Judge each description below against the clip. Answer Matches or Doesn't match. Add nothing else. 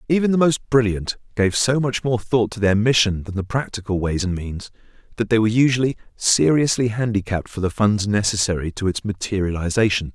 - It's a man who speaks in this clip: Matches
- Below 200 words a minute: Matches